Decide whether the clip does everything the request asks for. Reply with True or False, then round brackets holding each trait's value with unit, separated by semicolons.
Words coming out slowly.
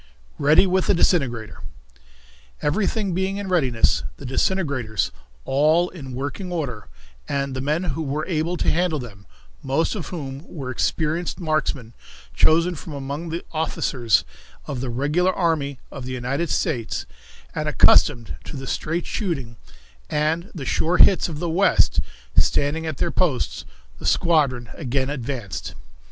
False (145 wpm)